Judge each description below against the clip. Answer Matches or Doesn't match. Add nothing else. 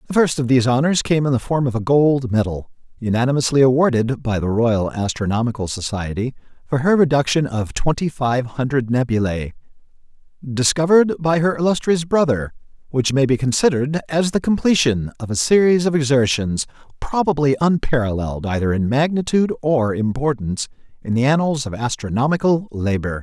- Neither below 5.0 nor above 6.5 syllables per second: Matches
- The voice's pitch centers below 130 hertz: Doesn't match